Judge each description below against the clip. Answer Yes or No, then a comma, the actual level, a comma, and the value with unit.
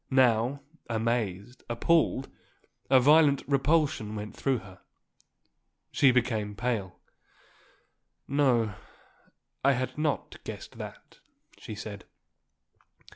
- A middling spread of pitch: Yes, average, 4.2 semitones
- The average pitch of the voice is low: Yes, low, 125 Hz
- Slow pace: Yes, slow, 90 wpm